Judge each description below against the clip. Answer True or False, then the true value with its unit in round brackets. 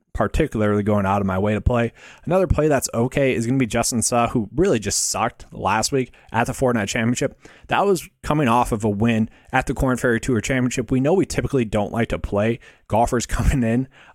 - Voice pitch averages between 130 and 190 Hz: False (120 Hz)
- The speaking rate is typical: False (220 wpm)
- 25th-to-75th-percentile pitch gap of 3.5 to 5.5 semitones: False (2.9 semitones)